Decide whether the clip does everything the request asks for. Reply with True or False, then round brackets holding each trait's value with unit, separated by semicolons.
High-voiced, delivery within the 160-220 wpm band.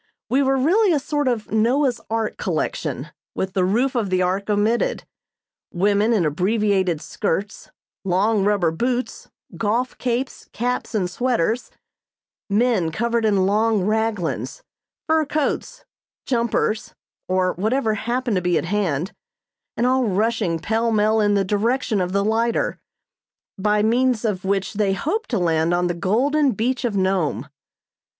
False (215 Hz; 145 wpm)